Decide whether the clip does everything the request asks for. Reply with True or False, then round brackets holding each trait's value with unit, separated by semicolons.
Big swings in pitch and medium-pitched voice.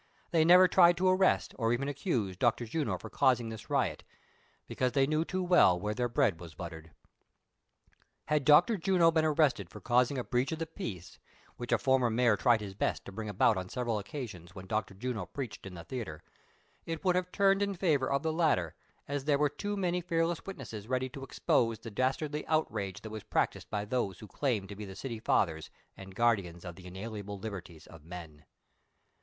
False (7.6 semitones; 120 Hz)